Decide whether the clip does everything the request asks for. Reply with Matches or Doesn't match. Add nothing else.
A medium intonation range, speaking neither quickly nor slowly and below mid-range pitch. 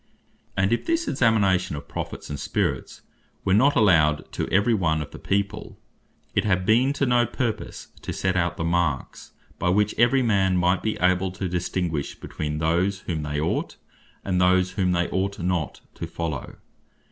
Matches